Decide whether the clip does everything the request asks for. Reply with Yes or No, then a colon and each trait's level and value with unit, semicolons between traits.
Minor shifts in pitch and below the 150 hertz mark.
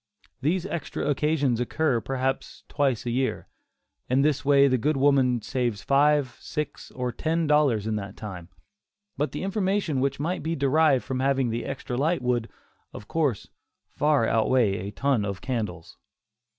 No: average, 3.8 semitones; low, 135 Hz